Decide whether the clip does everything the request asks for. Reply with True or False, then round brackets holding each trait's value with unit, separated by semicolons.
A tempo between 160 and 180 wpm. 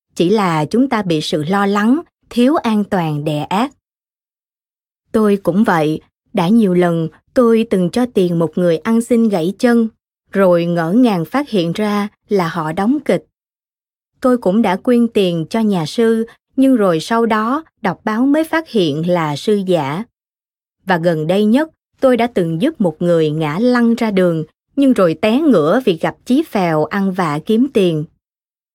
True (175 wpm)